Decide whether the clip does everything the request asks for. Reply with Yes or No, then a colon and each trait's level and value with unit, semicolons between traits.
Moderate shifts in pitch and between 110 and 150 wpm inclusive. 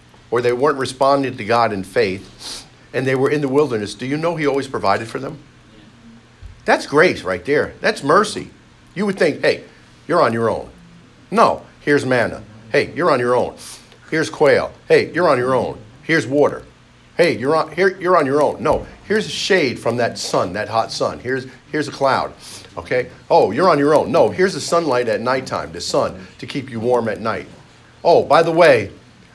No: average, 3.8 semitones; average, 200 wpm